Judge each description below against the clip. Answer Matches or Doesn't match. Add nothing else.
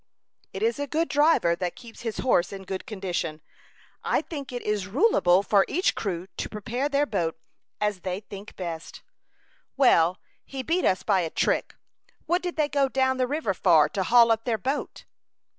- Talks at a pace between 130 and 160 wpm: Doesn't match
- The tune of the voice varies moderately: Doesn't match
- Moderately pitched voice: Doesn't match